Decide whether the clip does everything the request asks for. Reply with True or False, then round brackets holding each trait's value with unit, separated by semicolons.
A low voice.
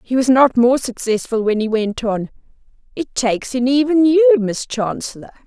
False (250 Hz)